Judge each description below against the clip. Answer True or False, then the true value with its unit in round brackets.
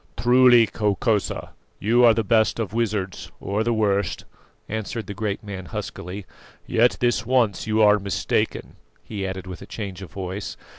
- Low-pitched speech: True (105 Hz)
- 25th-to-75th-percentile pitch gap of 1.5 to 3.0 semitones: True (2.7 semitones)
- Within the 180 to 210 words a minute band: False (160 wpm)